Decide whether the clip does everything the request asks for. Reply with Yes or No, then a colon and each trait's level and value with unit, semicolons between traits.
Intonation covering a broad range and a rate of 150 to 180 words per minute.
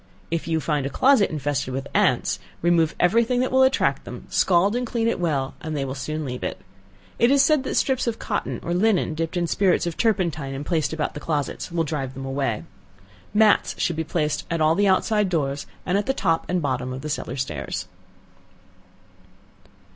No: wide, 6.0 semitones; fast, 205 wpm